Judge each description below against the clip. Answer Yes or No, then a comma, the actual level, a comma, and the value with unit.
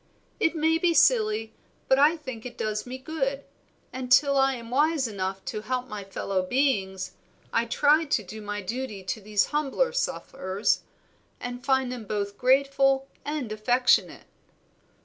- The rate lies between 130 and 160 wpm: Yes, average, 155 wpm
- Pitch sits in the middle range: No, very high, 250 Hz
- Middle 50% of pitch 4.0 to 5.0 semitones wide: Yes, average, 4.6 semitones